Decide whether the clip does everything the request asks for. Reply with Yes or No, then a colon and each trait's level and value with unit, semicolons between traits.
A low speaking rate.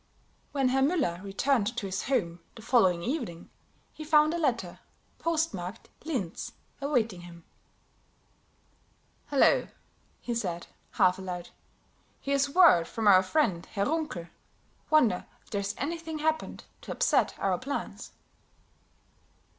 Yes: slow, 120 wpm